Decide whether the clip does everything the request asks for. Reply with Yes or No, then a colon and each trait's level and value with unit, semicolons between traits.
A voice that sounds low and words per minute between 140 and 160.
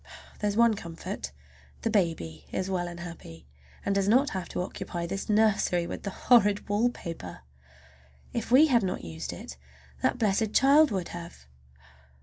No: high, 195 Hz; average, 155 wpm